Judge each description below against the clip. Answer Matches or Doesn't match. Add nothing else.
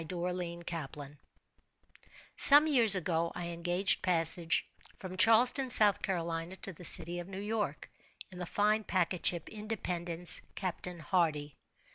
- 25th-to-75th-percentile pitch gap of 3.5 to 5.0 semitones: Doesn't match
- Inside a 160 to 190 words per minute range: Doesn't match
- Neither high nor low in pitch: Matches